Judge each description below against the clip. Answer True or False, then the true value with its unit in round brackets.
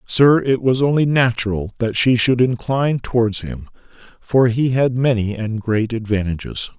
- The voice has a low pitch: True (120 Hz)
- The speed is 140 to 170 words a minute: True (160 wpm)